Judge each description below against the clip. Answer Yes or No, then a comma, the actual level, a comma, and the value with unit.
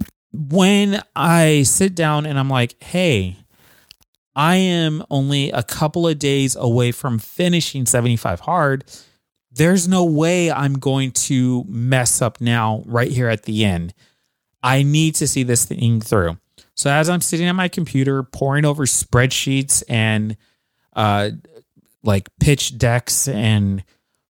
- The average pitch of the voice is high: No, low, 135 Hz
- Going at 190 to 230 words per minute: No, average, 140 wpm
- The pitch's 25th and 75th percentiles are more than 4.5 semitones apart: Yes, average, 5.0 semitones